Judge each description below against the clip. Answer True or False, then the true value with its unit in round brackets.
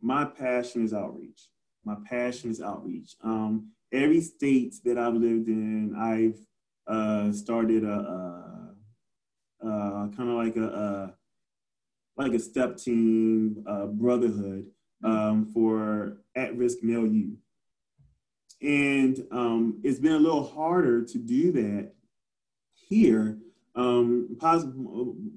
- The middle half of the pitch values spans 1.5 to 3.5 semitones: True (2.6 semitones)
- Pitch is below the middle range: True (115 Hz)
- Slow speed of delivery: True (120 wpm)